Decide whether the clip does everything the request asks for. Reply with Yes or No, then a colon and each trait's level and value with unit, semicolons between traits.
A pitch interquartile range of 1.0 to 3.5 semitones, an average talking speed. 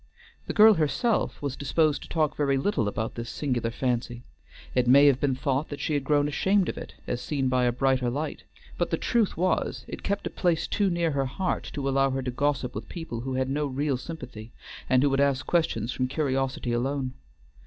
No: average, 3.1 semitones; fast, 215 wpm